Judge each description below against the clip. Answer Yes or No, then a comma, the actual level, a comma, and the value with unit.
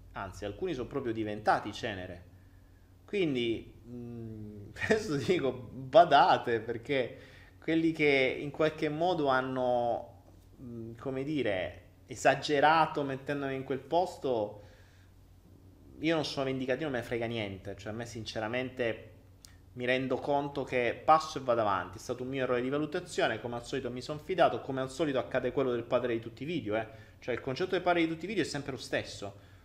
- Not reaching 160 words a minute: No, fast, 170 wpm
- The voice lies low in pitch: Yes, low, 125 Hz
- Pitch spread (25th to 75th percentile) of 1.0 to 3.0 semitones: No, average, 5.2 semitones